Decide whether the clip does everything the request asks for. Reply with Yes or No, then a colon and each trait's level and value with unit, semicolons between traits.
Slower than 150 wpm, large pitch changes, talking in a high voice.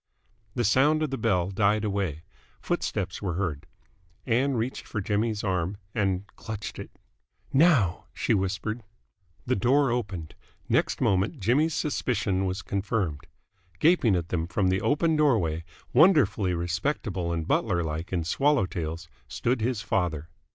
No: slow, 135 wpm; wide, 5.8 semitones; low, 100 Hz